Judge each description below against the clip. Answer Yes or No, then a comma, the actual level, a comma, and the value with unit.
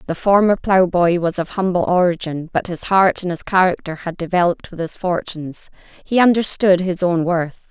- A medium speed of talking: Yes, average, 180 wpm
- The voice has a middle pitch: Yes, medium, 180 Hz